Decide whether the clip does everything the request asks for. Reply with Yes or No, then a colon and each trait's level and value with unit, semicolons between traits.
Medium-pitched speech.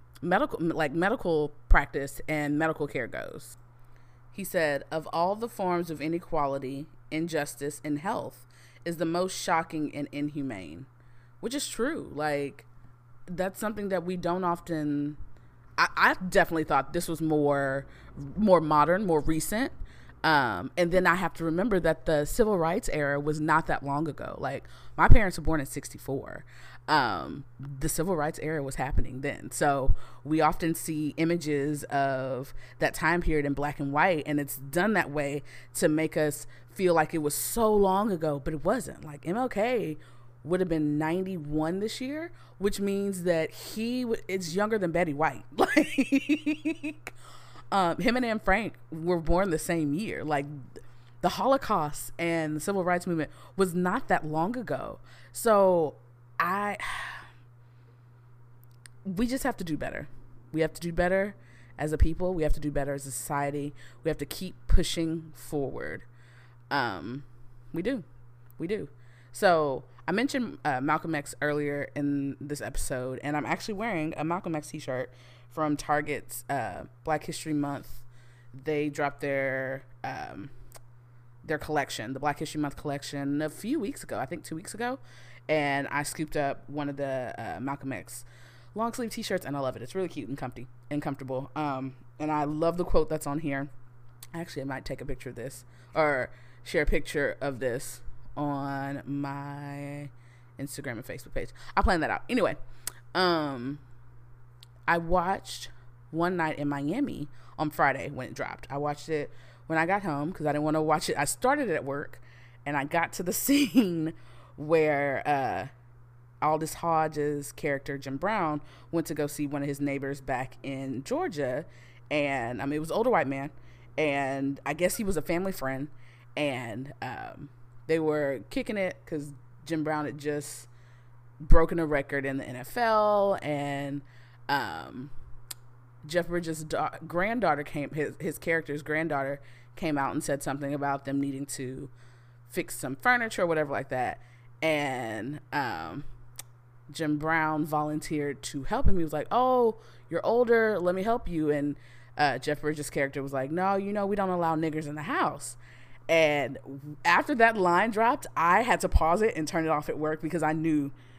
Yes: medium, 145 Hz